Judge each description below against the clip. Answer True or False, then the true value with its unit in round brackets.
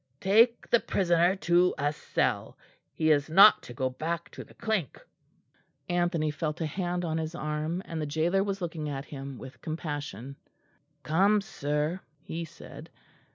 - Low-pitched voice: False (160 Hz)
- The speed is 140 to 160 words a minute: True (155 wpm)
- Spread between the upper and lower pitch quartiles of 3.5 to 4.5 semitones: False (3.1 semitones)